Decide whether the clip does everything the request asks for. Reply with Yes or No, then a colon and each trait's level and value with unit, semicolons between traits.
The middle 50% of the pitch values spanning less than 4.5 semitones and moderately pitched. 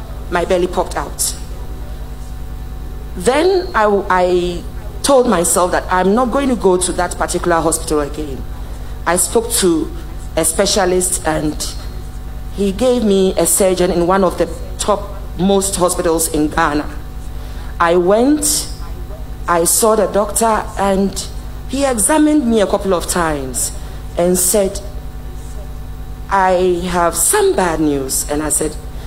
Yes: average, 3.8 semitones; medium, 180 Hz